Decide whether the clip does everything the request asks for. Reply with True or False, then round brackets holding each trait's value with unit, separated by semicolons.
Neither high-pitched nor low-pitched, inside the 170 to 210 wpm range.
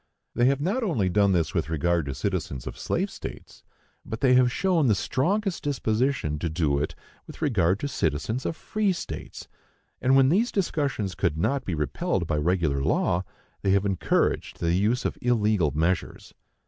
False (105 Hz; 175 wpm)